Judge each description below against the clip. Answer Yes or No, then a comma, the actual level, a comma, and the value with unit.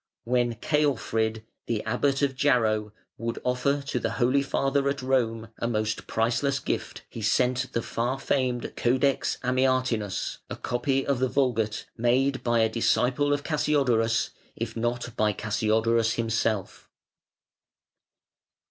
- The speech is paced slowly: Yes, slow, 130 wpm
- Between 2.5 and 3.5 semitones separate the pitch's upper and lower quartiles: Yes, average, 3.1 semitones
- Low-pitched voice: Yes, low, 120 Hz